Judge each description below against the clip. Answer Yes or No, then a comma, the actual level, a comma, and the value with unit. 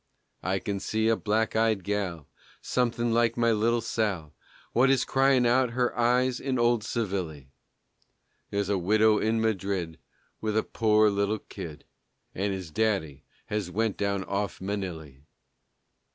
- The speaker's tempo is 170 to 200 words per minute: No, average, 145 wpm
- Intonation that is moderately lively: Yes, average, 3.3 semitones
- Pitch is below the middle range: Yes, low, 105 Hz